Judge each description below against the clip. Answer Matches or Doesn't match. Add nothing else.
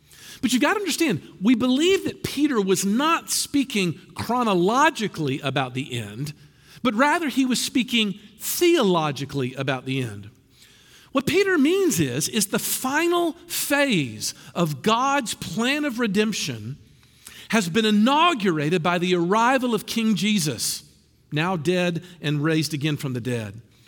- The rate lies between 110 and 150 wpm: Matches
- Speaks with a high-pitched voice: Matches